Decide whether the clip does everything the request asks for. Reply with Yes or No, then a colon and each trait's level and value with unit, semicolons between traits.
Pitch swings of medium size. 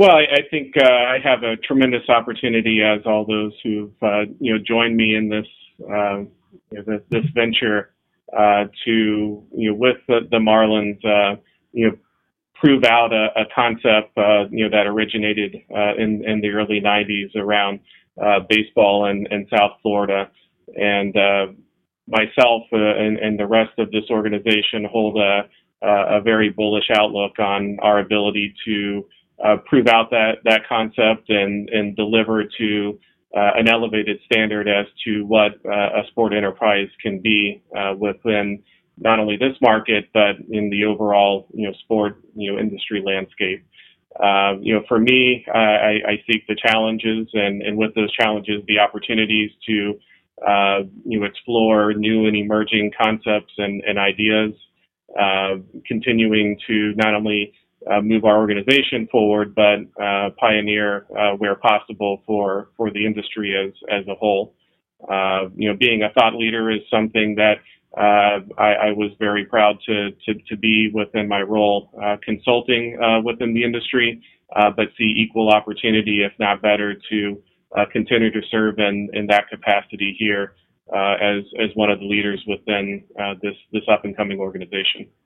No: narrow, 1.3 semitones